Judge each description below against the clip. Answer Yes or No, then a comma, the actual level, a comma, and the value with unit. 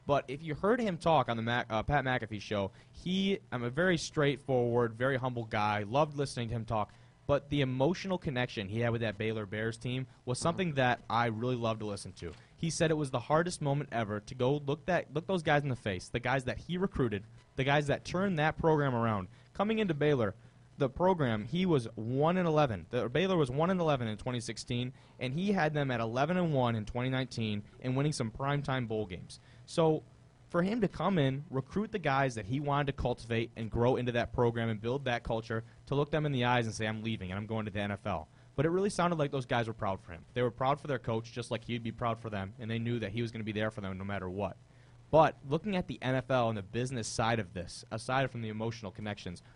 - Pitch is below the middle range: Yes, low, 125 Hz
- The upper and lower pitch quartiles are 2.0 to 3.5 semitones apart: No, average, 4.3 semitones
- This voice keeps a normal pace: No, fast, 250 wpm